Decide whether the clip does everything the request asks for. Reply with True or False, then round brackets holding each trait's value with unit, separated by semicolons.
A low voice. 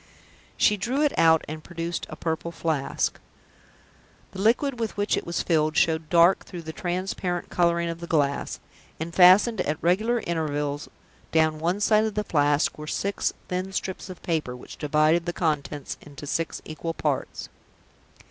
False (170 Hz)